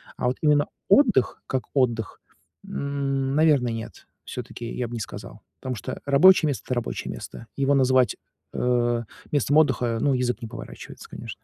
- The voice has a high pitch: No, low, 130 Hz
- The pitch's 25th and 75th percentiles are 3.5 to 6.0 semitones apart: No, average, 2.9 semitones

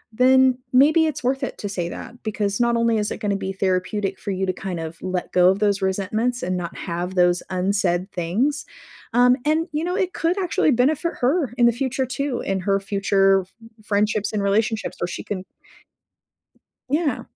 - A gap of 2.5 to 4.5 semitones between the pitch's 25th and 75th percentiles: No, wide, 5.4 semitones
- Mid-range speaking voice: No, high, 210 Hz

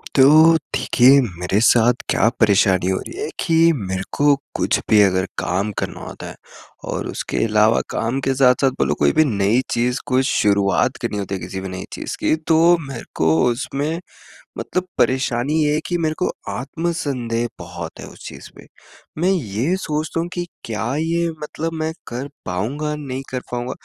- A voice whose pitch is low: Yes, low, 125 Hz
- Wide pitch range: Yes, wide, 6.4 semitones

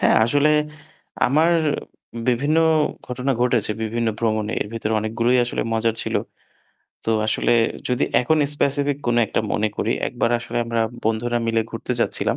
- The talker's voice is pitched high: No, low, 120 Hz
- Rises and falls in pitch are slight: Yes, narrow, 2.0 semitones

